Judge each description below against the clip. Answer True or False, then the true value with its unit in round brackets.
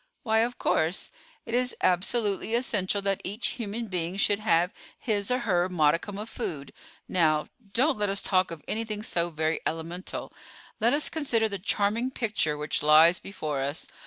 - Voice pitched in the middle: False (200 Hz)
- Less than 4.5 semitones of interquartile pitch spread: False (5.0 semitones)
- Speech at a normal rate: True (165 wpm)